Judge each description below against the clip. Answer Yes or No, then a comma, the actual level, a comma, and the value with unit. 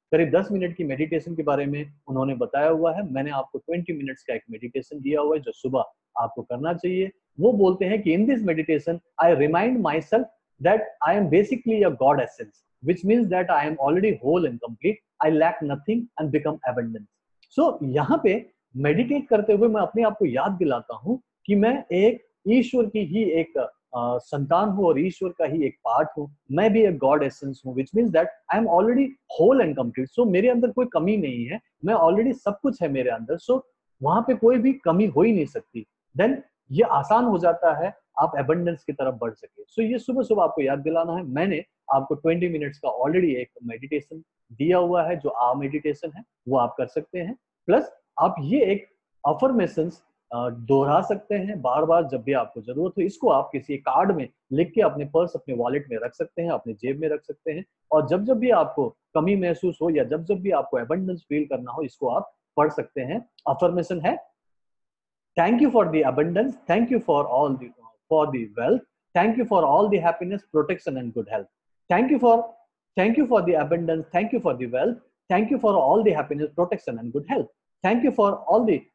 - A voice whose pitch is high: No, medium, 170 Hz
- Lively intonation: Yes, wide, 6.9 semitones